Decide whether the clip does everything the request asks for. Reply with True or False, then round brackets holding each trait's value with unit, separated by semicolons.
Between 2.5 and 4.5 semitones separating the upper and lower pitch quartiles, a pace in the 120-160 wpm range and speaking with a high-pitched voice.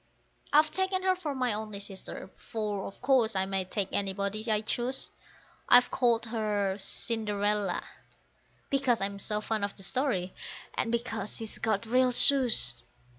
True (3.7 semitones; 150 wpm; 220 Hz)